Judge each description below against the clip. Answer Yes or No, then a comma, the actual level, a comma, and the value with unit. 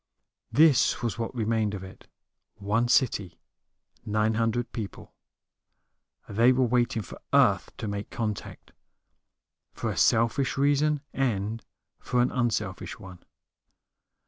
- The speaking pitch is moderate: No, low, 115 Hz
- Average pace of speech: No, slow, 120 wpm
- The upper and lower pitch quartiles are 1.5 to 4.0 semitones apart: Yes, average, 2.9 semitones